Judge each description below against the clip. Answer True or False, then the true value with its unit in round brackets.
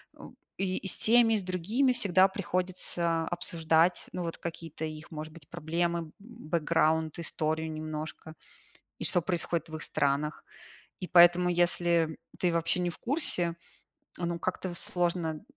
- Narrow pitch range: True (2.3 semitones)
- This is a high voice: False (170 Hz)